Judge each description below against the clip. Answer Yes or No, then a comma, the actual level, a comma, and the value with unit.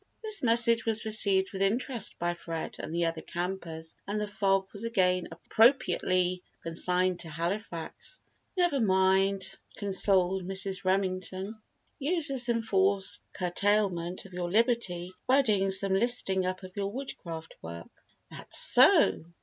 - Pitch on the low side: No, high, 190 Hz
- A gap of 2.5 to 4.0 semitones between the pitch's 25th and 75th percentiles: Yes, average, 3.3 semitones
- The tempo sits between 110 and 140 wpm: Yes, slow, 135 wpm